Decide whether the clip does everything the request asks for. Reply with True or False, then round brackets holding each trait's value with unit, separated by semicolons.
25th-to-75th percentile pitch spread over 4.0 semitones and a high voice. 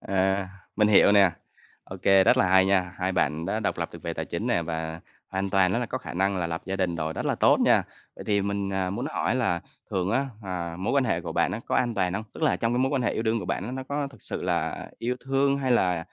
False (4.4 semitones; 95 Hz)